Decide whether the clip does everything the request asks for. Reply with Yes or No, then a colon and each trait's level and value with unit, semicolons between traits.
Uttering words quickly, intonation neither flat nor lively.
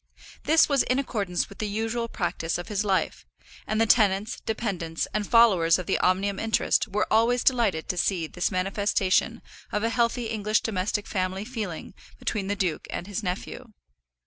No: average, 170 wpm; average, 3.4 semitones